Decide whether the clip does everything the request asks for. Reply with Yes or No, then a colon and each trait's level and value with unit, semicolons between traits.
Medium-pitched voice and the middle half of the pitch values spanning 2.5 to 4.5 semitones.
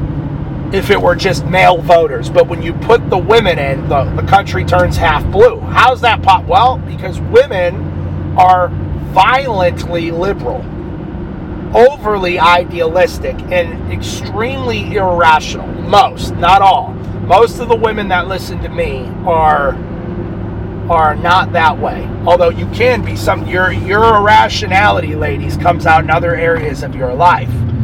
No: medium, 165 Hz; average, 5.0 semitones